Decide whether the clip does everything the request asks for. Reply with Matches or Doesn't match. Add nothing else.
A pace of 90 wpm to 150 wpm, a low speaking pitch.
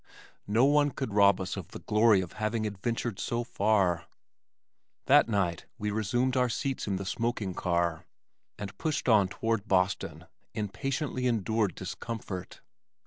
Matches